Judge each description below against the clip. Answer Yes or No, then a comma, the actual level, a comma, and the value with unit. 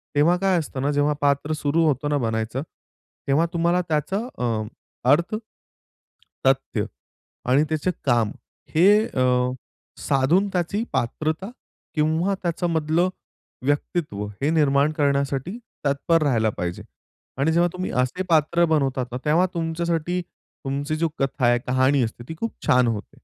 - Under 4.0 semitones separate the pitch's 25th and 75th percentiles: No, average, 4.3 semitones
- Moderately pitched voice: Yes, medium, 150 Hz